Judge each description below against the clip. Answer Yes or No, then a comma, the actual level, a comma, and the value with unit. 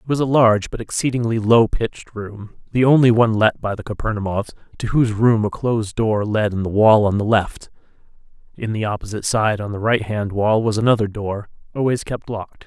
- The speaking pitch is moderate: No, low, 110 Hz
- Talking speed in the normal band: No, fast, 210 wpm